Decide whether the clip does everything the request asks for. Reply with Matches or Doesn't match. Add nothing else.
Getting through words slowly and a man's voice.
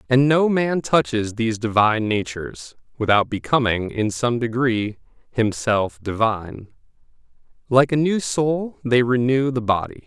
Matches